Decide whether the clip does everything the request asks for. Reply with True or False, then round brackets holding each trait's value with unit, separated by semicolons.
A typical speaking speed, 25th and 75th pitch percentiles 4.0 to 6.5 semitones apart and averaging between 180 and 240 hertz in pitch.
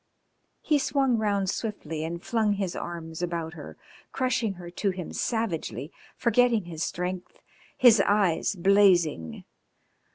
False (125 wpm; 4.7 semitones; 190 Hz)